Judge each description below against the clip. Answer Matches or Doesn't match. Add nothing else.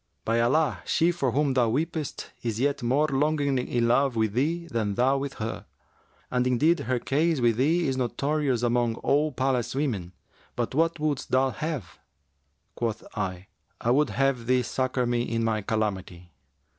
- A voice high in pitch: Doesn't match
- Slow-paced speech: Doesn't match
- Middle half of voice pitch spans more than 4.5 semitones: Doesn't match